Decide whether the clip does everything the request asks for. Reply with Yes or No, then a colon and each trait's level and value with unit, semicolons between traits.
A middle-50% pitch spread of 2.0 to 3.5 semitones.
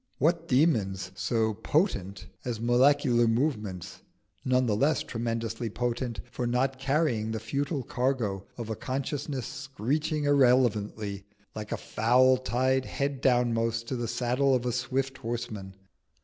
Yes: average, 3.2 semitones